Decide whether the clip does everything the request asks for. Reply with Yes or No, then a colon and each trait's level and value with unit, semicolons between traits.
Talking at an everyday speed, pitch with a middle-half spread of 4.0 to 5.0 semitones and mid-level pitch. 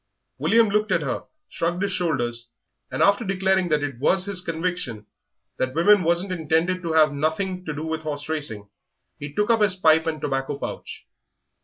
Yes: average, 180 wpm; average, 4.3 semitones; medium, 165 Hz